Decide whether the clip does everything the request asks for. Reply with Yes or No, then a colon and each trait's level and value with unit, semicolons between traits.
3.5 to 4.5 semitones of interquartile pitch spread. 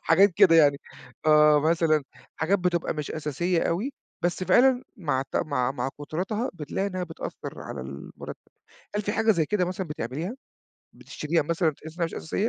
Yes: average, 4.0 semitones